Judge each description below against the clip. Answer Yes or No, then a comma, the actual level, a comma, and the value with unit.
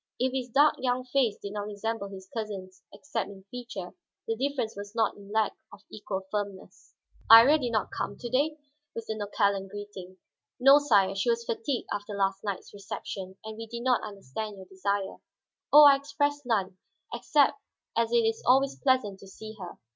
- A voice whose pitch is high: Yes, high, 220 Hz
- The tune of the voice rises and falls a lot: No, average, 3.8 semitones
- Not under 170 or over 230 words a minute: Yes, average, 185 wpm